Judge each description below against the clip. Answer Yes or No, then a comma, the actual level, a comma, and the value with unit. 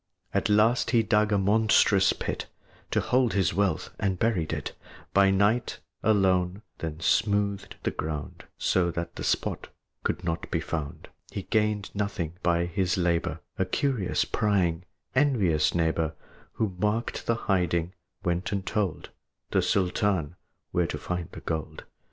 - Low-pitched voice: Yes, very low, 95 Hz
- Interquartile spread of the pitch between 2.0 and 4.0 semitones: Yes, average, 3.4 semitones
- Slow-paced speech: No, average, 150 wpm